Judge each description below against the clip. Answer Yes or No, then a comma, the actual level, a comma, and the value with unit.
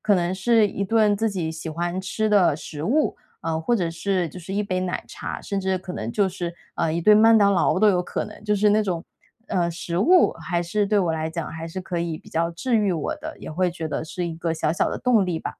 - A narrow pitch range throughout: No, average, 3.7 semitones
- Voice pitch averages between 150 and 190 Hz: Yes, medium, 185 Hz